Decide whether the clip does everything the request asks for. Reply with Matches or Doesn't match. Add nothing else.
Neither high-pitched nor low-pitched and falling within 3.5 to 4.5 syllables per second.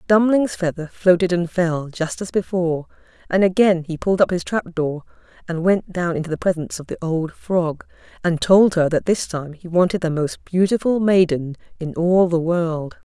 Doesn't match